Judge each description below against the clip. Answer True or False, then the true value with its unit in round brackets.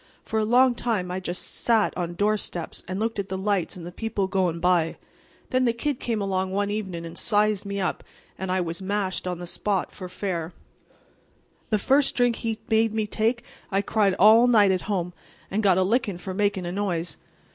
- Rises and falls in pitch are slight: False (3.1 semitones)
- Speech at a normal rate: False (210 wpm)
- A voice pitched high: True (200 Hz)